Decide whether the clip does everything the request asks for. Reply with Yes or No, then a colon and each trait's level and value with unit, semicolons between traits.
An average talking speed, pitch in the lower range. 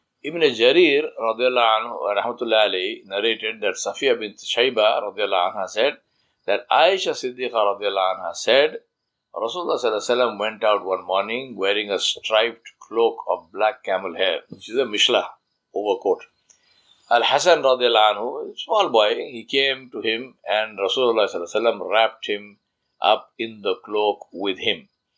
No: slow, 125 wpm; low, 125 Hz